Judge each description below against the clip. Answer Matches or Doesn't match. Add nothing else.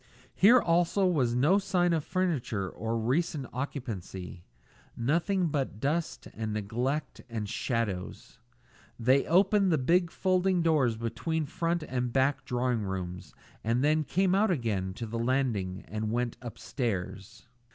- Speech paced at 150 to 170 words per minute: Doesn't match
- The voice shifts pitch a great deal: Matches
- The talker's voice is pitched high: Doesn't match